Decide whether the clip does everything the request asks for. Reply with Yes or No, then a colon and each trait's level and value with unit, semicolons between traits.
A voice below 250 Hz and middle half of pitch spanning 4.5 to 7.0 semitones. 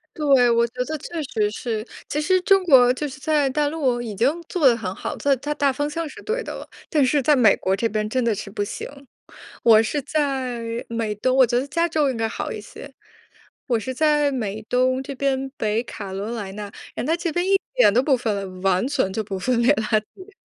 No: very high, 255 Hz; average, 5.1 semitones